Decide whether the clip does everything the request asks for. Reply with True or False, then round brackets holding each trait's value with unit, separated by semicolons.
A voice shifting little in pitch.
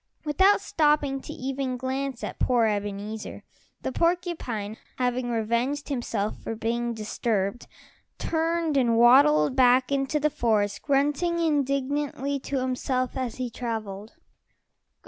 False (3.7 semitones)